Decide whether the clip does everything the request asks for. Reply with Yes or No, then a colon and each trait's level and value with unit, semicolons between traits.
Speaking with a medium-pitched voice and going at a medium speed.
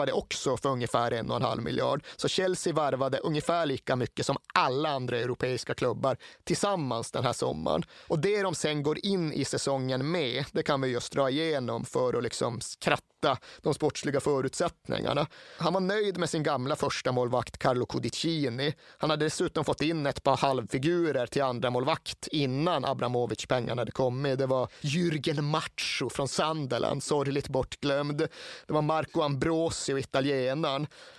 Yes: medium, 150 Hz; average, 160 wpm